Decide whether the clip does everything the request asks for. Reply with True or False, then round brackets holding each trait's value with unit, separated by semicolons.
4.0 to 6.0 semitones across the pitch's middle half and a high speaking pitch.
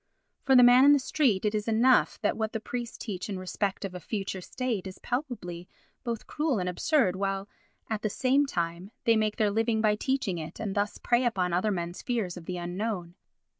True (4.6 semitones; 210 Hz)